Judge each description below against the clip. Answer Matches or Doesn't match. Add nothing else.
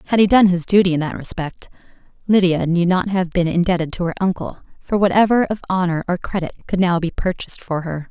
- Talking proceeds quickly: Matches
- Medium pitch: Matches